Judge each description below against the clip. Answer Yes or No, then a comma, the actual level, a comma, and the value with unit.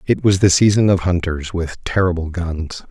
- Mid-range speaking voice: No, very low, 90 Hz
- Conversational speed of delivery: Yes, average, 185 wpm